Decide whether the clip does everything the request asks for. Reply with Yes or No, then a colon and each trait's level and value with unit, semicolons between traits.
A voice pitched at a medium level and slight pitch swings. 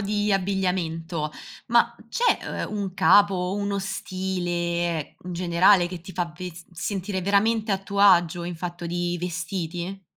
Yes: medium, 180 Hz; narrow, 2.3 semitones